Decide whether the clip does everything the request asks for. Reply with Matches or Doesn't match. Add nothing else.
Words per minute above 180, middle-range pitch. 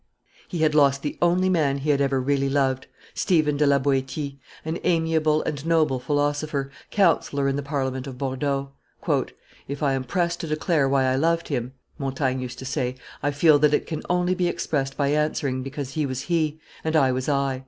Matches